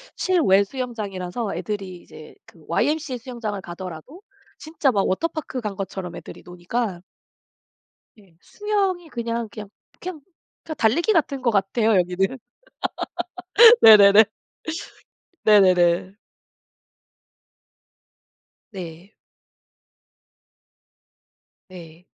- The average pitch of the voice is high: Yes, high, 210 Hz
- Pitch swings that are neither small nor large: No, wide, 5.8 semitones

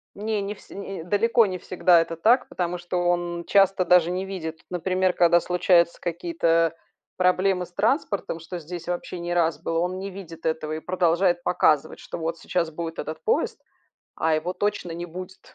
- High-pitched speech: No, medium, 175 Hz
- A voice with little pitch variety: Yes, narrow, 1.9 semitones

